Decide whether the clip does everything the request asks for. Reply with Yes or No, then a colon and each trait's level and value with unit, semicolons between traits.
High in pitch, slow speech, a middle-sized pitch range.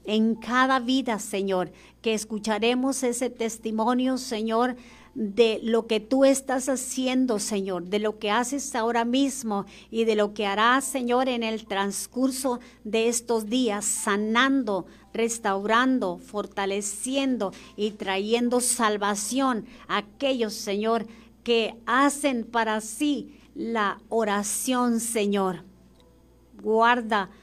Yes: high, 225 Hz; slow, 110 wpm; average, 3.1 semitones